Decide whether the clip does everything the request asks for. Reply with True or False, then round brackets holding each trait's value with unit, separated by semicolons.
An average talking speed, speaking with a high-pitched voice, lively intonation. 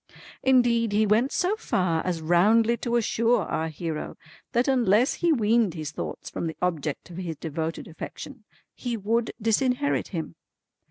True (155 wpm; 210 Hz; 6.2 semitones)